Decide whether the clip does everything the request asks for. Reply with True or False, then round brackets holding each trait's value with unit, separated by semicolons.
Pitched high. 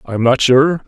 False (135 Hz)